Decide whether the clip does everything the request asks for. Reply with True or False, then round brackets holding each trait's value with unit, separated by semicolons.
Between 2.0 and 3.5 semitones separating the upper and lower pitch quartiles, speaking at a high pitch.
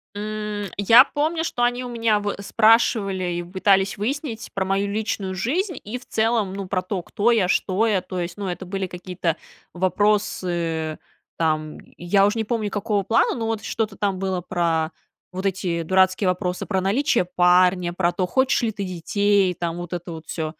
True (3.2 semitones; 195 Hz)